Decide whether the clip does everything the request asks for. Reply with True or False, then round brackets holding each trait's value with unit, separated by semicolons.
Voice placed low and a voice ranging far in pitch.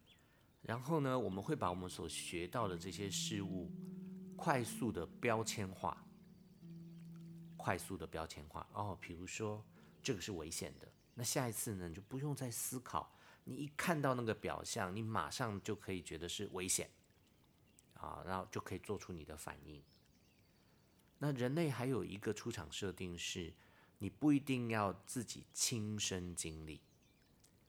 True (105 Hz; 6.4 semitones)